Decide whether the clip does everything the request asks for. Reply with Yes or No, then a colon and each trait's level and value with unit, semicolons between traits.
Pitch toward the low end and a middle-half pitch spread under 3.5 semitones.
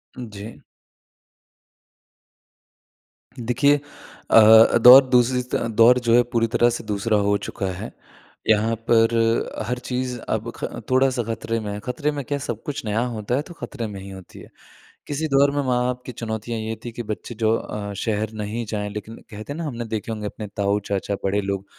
Yes: low, 115 Hz; average, 2.9 semitones